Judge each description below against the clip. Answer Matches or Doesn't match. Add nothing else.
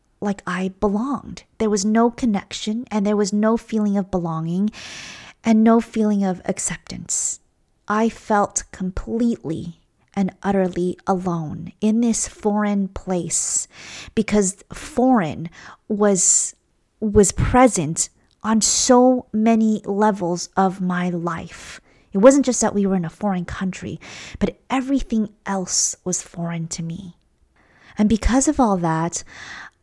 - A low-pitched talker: Doesn't match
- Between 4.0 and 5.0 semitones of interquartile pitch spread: Doesn't match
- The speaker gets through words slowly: Matches